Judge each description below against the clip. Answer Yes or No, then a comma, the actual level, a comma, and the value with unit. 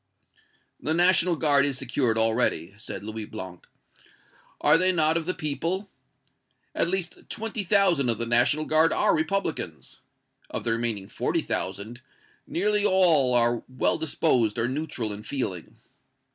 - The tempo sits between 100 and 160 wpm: Yes, average, 145 wpm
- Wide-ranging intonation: Yes, wide, 7.0 semitones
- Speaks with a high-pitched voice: No, medium, 140 Hz